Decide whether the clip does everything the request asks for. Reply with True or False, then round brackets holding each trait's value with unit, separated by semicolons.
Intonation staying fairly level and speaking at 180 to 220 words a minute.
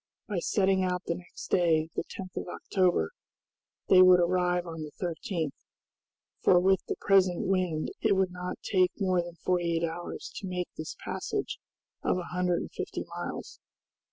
False (1.3 semitones; 170 wpm)